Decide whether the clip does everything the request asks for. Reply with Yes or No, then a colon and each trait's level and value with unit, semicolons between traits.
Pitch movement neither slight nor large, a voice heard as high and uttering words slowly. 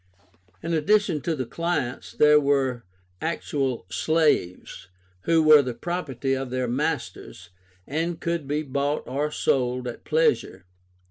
No: average, 4.0 semitones; medium, 145 Hz; slow, 130 wpm